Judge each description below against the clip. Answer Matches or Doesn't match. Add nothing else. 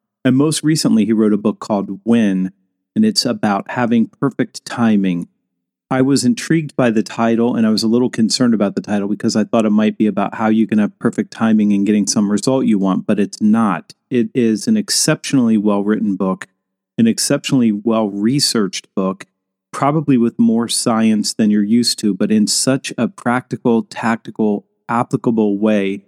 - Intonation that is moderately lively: Matches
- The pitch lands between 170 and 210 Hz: Doesn't match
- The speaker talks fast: Doesn't match